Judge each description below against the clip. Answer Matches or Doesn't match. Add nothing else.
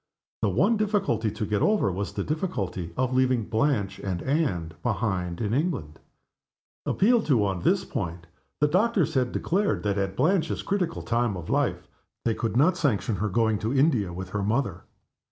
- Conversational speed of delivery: Matches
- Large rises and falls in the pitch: Matches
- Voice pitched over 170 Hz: Doesn't match